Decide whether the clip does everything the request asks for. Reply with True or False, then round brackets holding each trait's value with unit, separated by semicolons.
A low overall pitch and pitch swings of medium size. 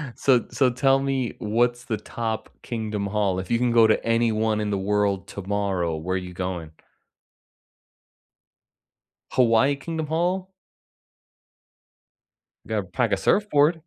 True (110 Hz; 4.7 semitones)